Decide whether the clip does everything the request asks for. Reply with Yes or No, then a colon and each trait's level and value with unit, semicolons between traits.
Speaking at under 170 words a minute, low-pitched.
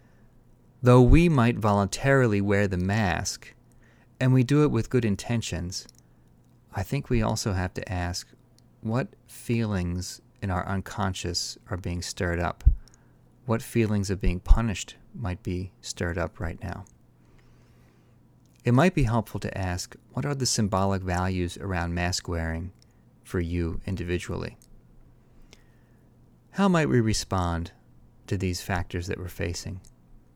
Yes: slow, 135 wpm; low, 100 Hz